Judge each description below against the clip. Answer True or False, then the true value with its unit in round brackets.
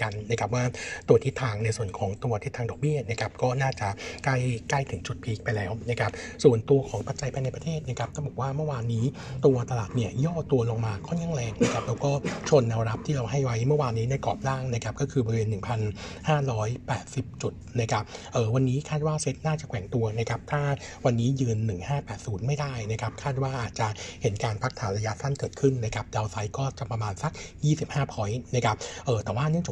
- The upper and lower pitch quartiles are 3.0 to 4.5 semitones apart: True (3.6 semitones)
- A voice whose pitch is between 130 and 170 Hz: False (120 Hz)